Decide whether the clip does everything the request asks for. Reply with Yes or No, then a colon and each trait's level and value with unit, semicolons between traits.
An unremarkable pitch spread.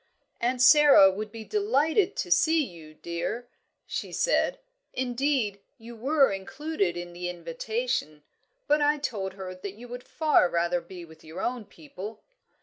No: wide, 7.4 semitones